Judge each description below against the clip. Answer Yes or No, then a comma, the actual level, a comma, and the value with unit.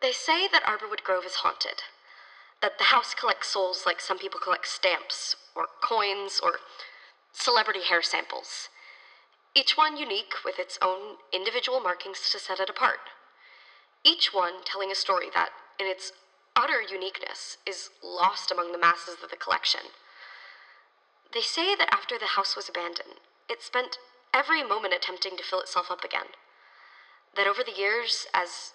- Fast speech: No, average, 160 wpm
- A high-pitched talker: Yes, high, 215 Hz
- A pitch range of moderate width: No, wide, 8.5 semitones